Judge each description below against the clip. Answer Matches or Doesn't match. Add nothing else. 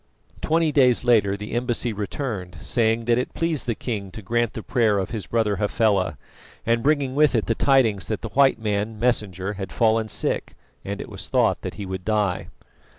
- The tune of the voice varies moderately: Matches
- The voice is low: Matches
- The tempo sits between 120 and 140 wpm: Doesn't match